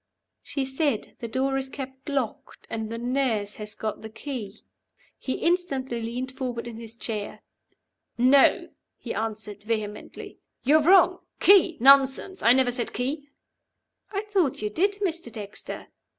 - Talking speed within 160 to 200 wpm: No, average, 145 wpm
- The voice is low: No, very high, 255 Hz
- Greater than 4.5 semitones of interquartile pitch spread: No, average, 4.0 semitones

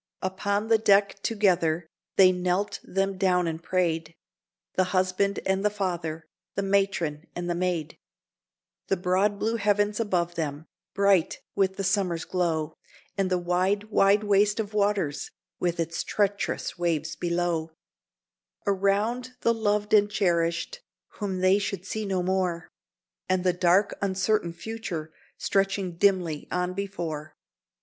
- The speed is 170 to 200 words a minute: No, slow, 135 wpm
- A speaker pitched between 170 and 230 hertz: Yes, medium, 185 Hz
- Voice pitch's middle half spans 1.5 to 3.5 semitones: Yes, average, 2.7 semitones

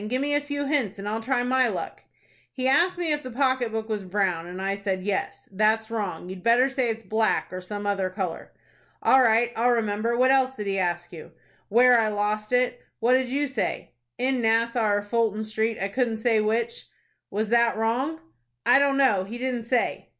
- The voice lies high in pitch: Yes, high, 225 Hz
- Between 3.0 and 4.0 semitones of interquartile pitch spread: Yes, average, 3.7 semitones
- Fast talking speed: Yes, fast, 210 wpm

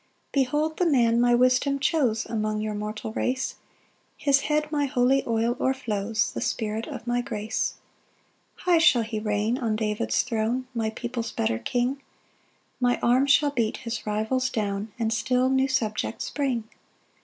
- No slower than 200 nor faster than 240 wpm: No, average, 160 wpm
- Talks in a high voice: Yes, high, 240 Hz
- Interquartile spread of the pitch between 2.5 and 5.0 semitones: Yes, average, 3.4 semitones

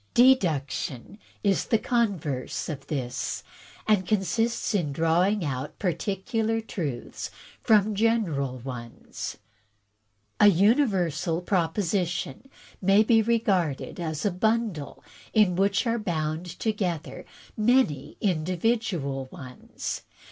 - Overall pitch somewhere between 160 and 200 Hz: Yes, medium, 185 Hz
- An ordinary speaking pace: No, slow, 105 wpm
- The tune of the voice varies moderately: No, wide, 5.9 semitones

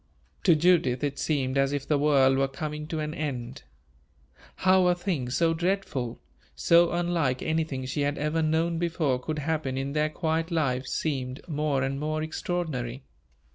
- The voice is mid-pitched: Yes, medium, 150 Hz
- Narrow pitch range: No, average, 3.4 semitones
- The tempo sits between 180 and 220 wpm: No, average, 165 wpm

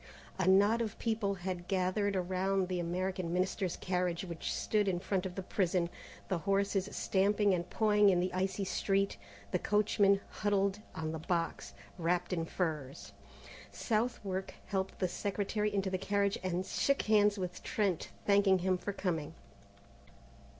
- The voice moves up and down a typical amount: No, narrow, 2.0 semitones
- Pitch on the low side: No, high, 190 Hz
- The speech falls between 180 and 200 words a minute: No, average, 150 wpm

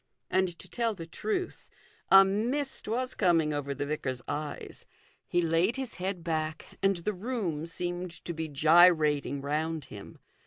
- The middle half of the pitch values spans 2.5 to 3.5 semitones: No, average, 4.2 semitones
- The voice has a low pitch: No, medium, 170 Hz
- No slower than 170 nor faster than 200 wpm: No, average, 155 wpm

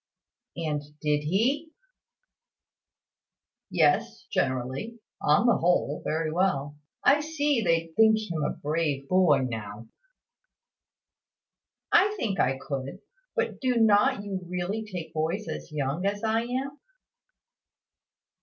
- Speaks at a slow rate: Yes, slow, 115 wpm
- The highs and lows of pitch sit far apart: Yes, wide, 7.0 semitones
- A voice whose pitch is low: No, medium, 180 Hz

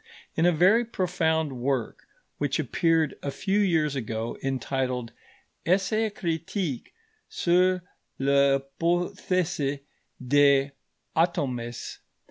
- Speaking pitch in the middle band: Yes, medium, 150 Hz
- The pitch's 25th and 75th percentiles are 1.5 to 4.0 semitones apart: No, average, 4.7 semitones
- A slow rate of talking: Yes, slow, 95 wpm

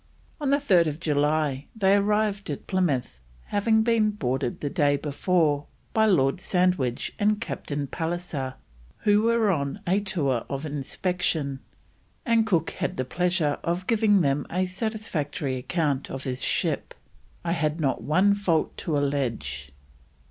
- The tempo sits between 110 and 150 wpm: Yes, average, 140 wpm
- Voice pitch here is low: No, medium, 165 Hz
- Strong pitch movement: Yes, wide, 6.1 semitones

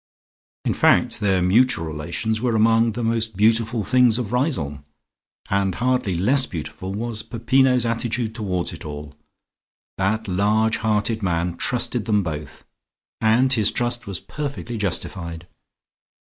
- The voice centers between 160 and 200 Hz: No, low, 110 Hz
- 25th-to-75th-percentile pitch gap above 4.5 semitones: No, average, 4.2 semitones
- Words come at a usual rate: No, slow, 130 wpm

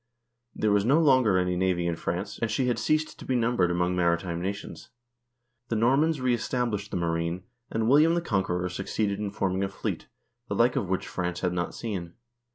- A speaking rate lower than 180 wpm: No, average, 190 wpm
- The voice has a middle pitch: No, low, 100 Hz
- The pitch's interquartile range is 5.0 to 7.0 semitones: Yes, wide, 5.4 semitones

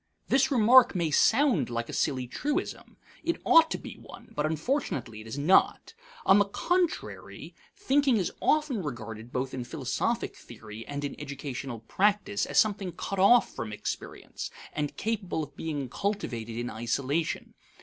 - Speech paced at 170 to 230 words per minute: No, average, 155 wpm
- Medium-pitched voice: Yes, medium, 155 Hz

